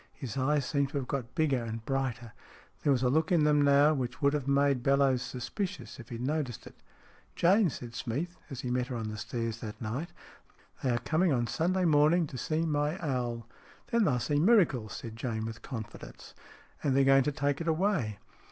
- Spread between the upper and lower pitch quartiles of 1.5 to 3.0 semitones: No, average, 4.1 semitones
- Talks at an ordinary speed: No, fast, 215 wpm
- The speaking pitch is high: No, low, 135 Hz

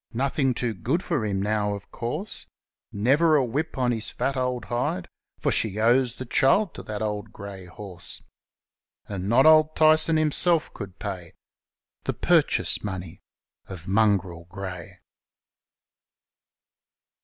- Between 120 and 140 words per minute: Yes, slow, 135 wpm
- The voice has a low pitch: Yes, low, 110 Hz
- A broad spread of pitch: Yes, wide, 5.8 semitones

